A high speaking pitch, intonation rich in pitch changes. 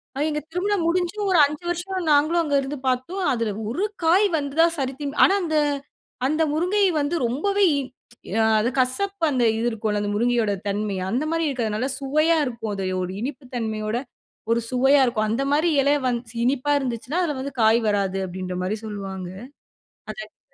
Yes: very high, 270 Hz; wide, 6.4 semitones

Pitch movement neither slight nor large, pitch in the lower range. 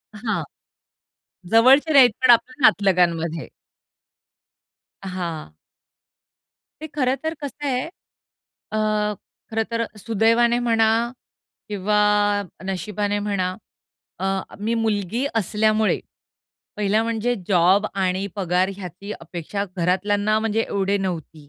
No: average, 3.4 semitones; high, 210 Hz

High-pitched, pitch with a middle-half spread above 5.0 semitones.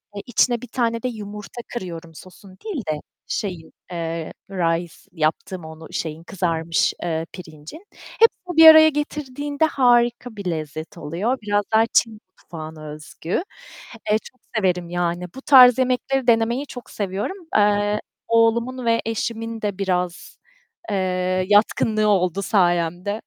Yes: high, 205 Hz; wide, 5.6 semitones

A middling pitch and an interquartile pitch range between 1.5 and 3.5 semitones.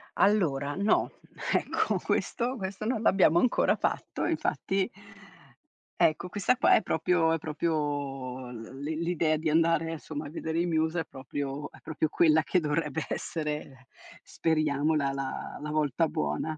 Yes: medium, 155 Hz; average, 2.8 semitones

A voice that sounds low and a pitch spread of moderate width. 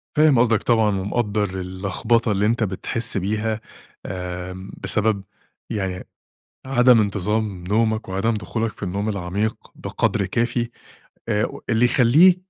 Yes: low, 110 Hz; average, 3.0 semitones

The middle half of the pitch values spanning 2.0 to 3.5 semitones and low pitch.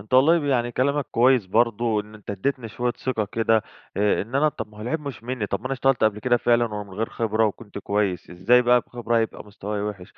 Yes: average, 3.1 semitones; low, 115 Hz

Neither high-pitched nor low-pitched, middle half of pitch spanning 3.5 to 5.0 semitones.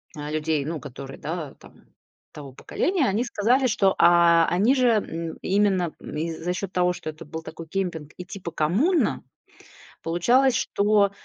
Yes: medium, 175 Hz; average, 4.4 semitones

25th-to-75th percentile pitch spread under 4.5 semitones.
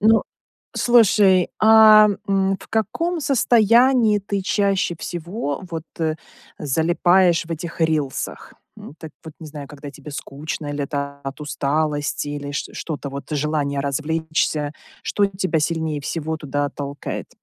No: average, 5.2 semitones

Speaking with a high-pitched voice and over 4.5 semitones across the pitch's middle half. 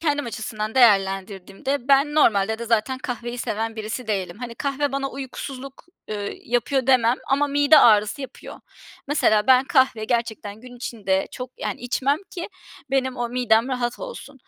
No: high, 245 Hz; average, 3.8 semitones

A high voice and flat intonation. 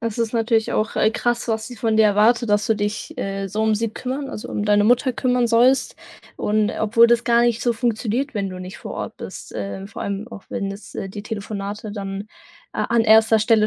Yes: high, 220 Hz; narrow, 2.3 semitones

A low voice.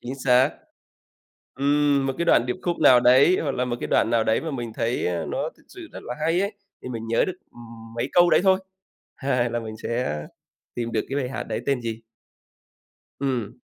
Yes: low, 125 Hz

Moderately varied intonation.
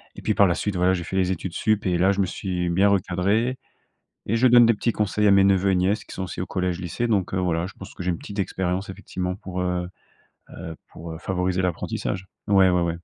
No: narrow, 1.8 semitones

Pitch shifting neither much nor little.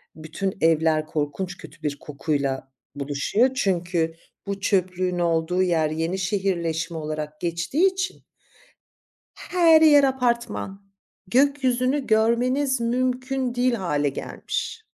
No: wide, 7.8 semitones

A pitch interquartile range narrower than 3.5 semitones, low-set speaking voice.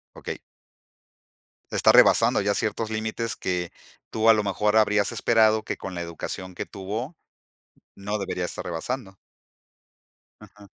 Yes: narrow, 2.5 semitones; low, 105 Hz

